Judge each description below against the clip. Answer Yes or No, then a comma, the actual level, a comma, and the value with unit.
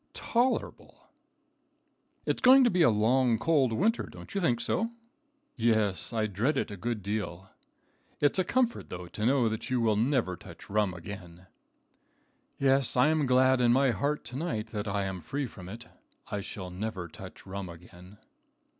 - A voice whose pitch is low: Yes, low, 115 Hz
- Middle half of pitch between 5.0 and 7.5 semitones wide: Yes, wide, 5.5 semitones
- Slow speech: No, average, 170 wpm